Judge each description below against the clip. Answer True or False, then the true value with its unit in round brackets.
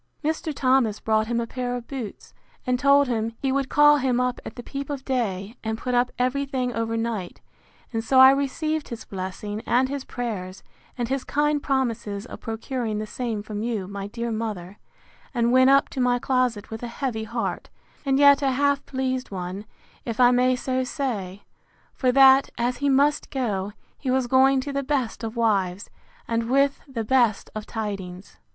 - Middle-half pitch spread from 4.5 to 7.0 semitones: False (3.4 semitones)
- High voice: True (245 Hz)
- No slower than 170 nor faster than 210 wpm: True (190 wpm)